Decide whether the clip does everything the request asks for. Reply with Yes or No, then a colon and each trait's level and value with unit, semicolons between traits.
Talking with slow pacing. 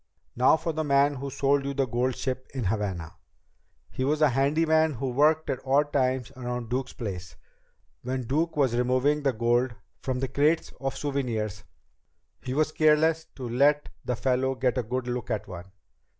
No: average, 180 wpm